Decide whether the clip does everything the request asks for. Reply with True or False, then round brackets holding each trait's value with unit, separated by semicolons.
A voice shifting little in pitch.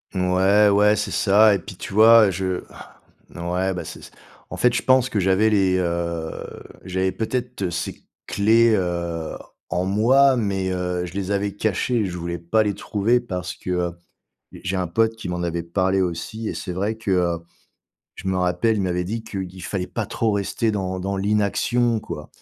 False (3.3 semitones)